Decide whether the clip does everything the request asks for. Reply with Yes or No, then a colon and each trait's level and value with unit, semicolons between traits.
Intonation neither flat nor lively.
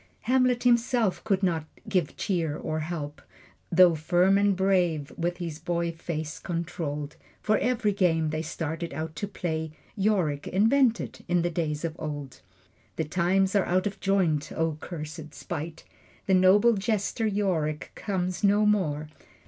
Yes: average, 3.9 semitones